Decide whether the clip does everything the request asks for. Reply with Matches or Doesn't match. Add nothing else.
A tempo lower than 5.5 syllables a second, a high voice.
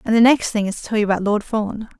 Doesn't match